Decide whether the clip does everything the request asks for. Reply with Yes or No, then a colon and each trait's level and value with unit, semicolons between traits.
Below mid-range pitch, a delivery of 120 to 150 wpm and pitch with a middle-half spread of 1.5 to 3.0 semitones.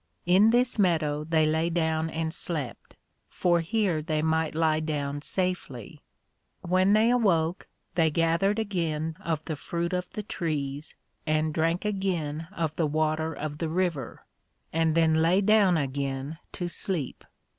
No: medium, 160 Hz; average, 145 wpm; average, 2.7 semitones